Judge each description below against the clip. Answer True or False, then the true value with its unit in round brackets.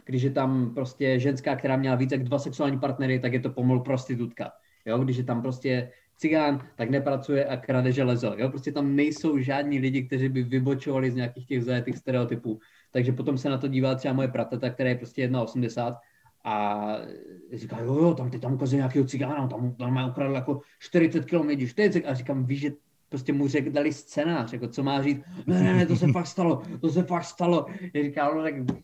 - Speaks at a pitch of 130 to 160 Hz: True (135 Hz)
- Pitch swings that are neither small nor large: False (2.3 semitones)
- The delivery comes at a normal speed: False (215 wpm)